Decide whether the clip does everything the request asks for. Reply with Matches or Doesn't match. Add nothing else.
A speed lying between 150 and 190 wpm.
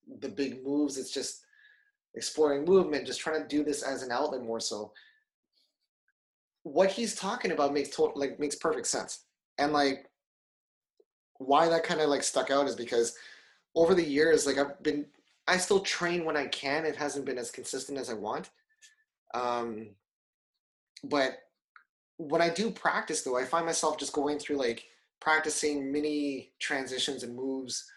Matches